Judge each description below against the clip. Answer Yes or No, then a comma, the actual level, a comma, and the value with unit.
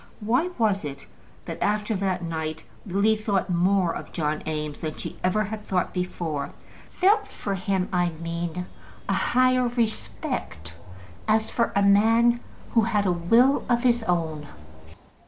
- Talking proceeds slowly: No, average, 150 wpm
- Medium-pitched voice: No, high, 195 Hz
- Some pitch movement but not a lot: Yes, average, 4.8 semitones